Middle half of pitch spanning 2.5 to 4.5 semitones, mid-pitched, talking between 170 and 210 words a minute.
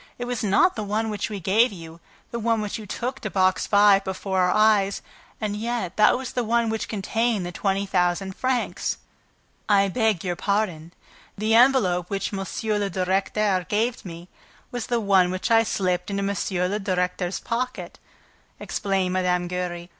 No: average, 3.3 semitones; high, 200 Hz; average, 175 wpm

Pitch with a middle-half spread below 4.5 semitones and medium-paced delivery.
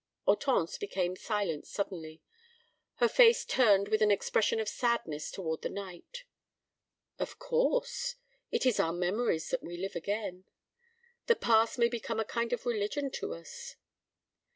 No: average, 5.1 semitones; average, 150 wpm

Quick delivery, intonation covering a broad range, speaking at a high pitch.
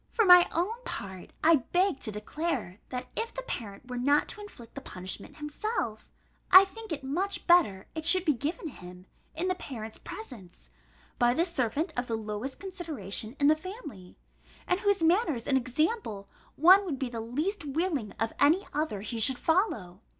No: average, 180 wpm; wide, 8.0 semitones; very high, 290 Hz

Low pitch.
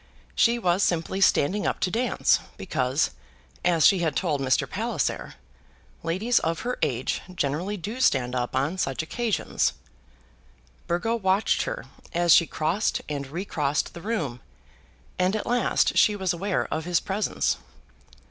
No: medium, 175 Hz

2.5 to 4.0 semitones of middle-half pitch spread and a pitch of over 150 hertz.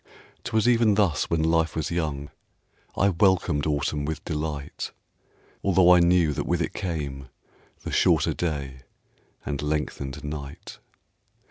No: average, 3.4 semitones; very low, 80 Hz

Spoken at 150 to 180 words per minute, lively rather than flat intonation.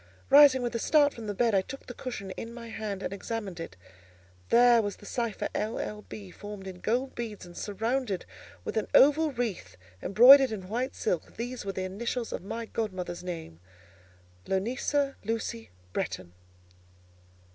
No: average, 165 wpm; average, 4.4 semitones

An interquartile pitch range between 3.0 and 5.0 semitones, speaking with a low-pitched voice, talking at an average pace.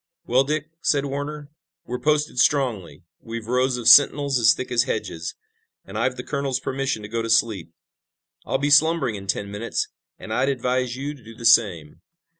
Yes: average, 3.7 semitones; low, 125 Hz; average, 185 wpm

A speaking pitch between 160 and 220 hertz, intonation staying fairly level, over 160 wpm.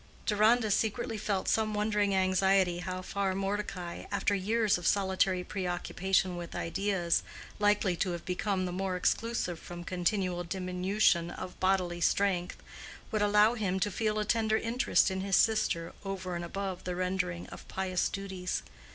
No: high, 190 Hz; narrow, 2.3 semitones; average, 150 wpm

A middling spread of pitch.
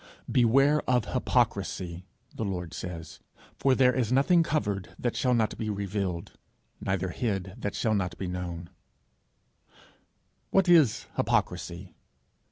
No: wide, 5.8 semitones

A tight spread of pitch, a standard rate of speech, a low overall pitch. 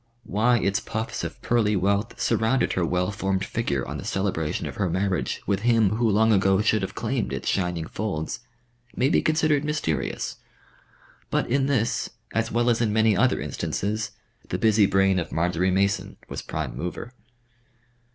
No: average, 3.3 semitones; average, 170 wpm; low, 105 Hz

